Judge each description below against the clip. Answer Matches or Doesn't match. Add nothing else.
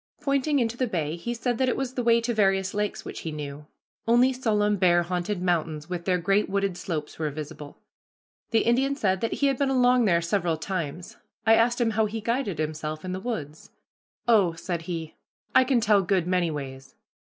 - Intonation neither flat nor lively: Doesn't match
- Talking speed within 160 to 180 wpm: Doesn't match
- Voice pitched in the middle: Doesn't match